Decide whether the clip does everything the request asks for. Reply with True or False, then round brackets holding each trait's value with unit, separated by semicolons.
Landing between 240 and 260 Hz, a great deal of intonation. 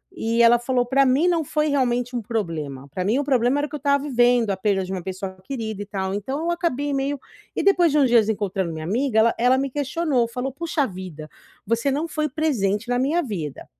True (245 Hz; 5.7 semitones)